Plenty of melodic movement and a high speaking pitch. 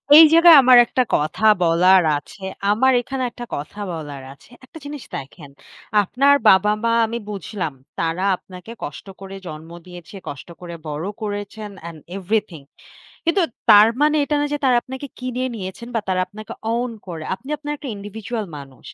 Yes: wide, 6.4 semitones; high, 205 Hz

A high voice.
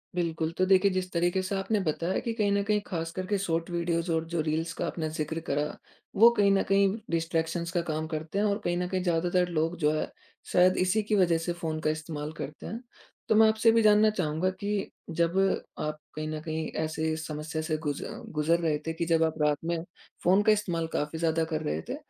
No: medium, 170 Hz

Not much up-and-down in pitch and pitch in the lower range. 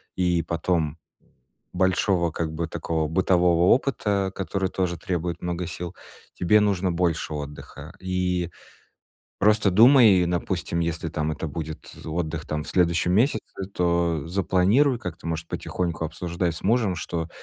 Yes: narrow, 2.2 semitones; very low, 90 Hz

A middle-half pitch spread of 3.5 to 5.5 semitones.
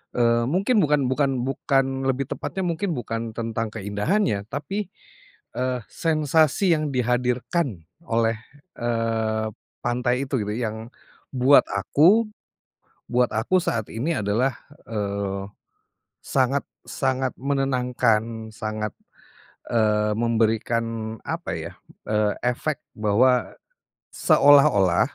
Yes: average, 3.9 semitones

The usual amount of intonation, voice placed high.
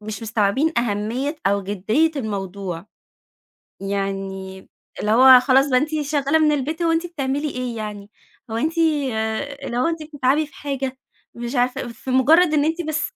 No: wide, 6.1 semitones; very high, 255 Hz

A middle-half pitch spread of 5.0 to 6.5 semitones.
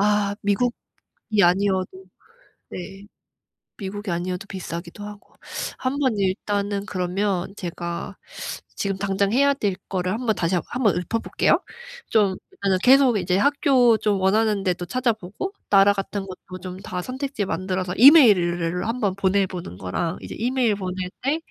No: average, 3.2 semitones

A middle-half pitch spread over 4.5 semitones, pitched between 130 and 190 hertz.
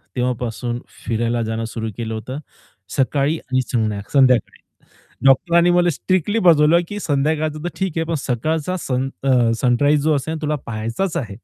Yes: average, 5.1 semitones; low, 135 Hz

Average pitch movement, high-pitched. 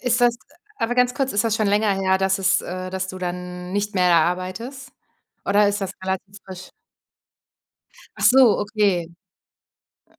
Yes: average, 3.0 semitones; high, 195 Hz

